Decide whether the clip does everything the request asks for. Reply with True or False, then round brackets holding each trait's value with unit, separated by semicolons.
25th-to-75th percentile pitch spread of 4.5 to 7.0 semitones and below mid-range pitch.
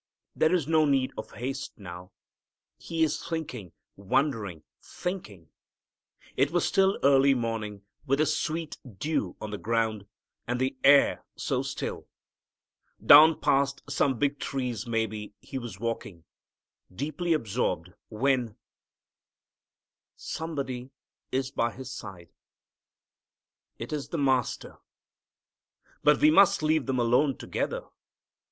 True (5.0 semitones; 130 Hz)